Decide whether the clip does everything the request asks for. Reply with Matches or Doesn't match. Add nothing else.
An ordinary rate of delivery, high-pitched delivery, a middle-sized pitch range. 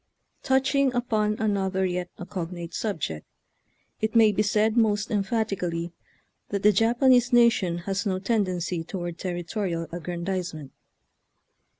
Doesn't match